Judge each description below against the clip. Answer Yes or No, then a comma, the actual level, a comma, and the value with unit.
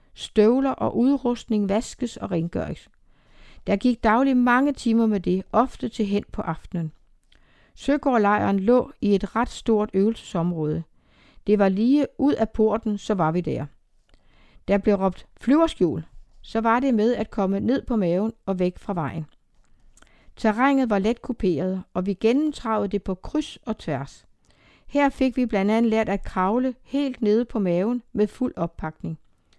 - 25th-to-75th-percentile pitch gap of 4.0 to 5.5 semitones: Yes, average, 4.5 semitones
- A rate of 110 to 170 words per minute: Yes, average, 160 wpm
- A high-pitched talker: Yes, high, 215 Hz